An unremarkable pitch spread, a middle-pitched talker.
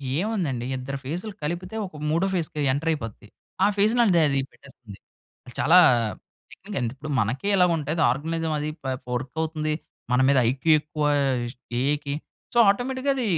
Yes: average, 5.0 semitones; medium, 155 Hz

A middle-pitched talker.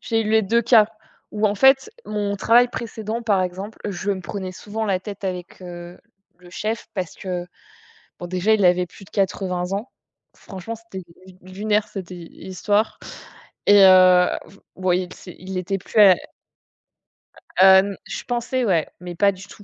No: high, 195 Hz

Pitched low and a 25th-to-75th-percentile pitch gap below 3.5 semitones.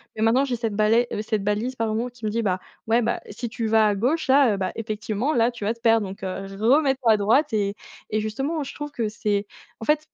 No: high, 225 Hz; average, 2.8 semitones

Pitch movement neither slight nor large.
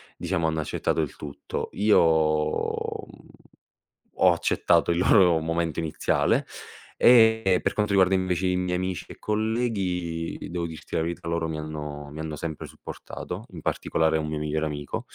Yes: average, 3.0 semitones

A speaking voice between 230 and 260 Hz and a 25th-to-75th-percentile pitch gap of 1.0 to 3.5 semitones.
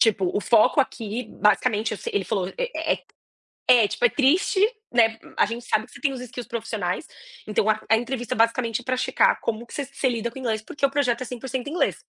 Yes: high, 235 Hz; average, 3.1 semitones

